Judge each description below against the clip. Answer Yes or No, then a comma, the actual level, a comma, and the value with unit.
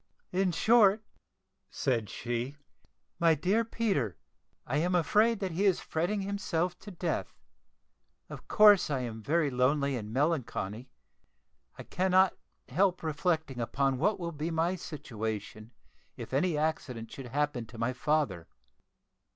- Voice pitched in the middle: Yes, medium, 155 Hz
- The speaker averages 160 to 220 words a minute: No, slow, 135 wpm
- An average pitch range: No, wide, 6.5 semitones